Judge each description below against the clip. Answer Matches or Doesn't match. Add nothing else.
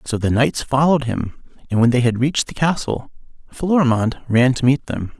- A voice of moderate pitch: Doesn't match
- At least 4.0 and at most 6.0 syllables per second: Matches